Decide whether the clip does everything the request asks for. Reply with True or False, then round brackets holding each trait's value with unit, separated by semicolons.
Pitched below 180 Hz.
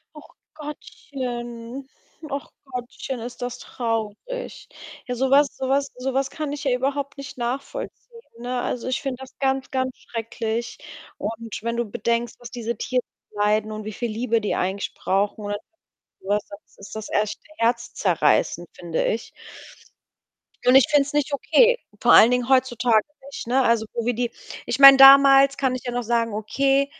False (245 Hz)